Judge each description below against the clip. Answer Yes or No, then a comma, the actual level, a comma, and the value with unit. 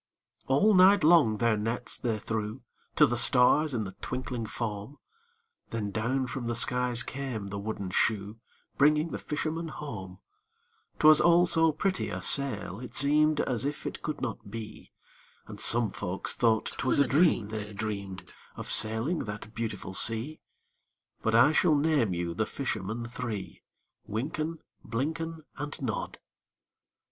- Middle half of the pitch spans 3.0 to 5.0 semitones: No, wide, 5.6 semitones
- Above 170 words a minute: No, average, 150 wpm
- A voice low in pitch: Yes, low, 120 Hz